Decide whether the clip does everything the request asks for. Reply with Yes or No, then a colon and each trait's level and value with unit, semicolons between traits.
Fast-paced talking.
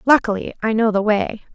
No: average, 195 wpm